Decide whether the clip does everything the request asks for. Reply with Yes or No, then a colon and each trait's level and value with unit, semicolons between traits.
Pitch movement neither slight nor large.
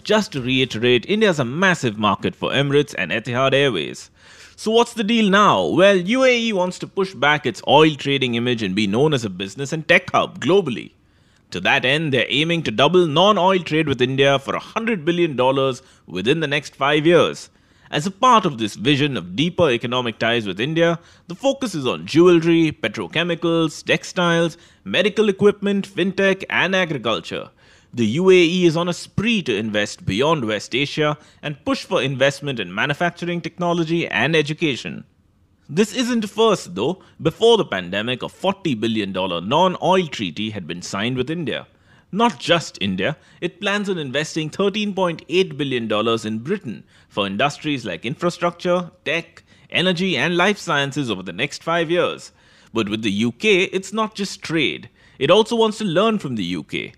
No: wide, 5.9 semitones